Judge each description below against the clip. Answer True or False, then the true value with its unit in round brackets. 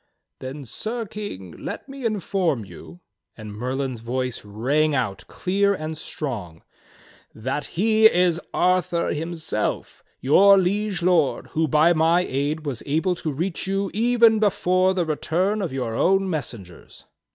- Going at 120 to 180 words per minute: True (140 wpm)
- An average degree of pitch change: False (6.6 semitones)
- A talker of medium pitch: True (165 Hz)